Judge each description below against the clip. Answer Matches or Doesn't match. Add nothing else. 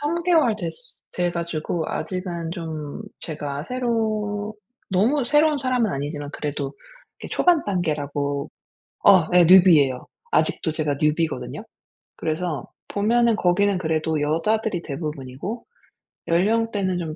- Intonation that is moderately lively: Doesn't match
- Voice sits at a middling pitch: Matches